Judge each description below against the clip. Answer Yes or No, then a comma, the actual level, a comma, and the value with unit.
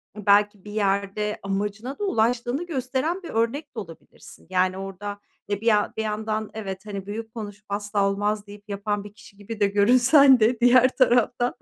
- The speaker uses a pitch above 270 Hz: No, high, 210 Hz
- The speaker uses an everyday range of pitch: Yes, average, 3.1 semitones